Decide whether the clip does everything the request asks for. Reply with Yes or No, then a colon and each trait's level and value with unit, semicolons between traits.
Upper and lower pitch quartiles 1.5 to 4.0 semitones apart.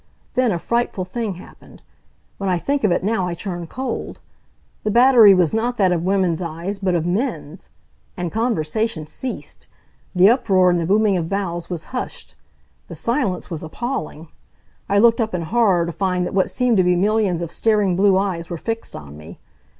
No: average, 4.4 semitones